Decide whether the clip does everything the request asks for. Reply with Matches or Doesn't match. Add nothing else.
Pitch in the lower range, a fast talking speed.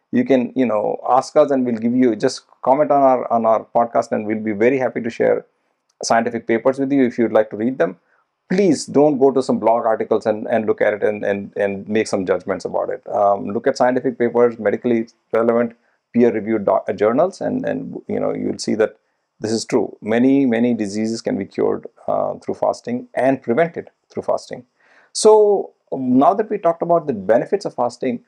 Matches